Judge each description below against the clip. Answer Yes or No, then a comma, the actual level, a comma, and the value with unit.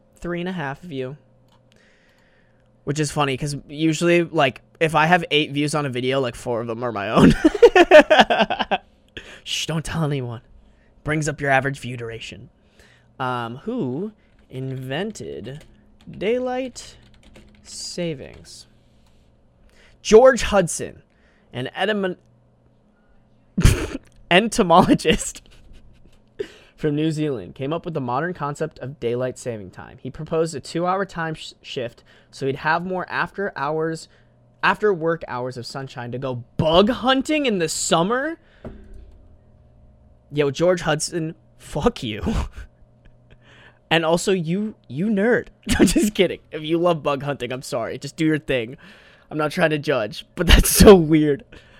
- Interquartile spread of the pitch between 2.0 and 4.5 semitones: No, wide, 5.6 semitones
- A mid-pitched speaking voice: Yes, medium, 155 Hz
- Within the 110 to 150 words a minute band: Yes, average, 140 wpm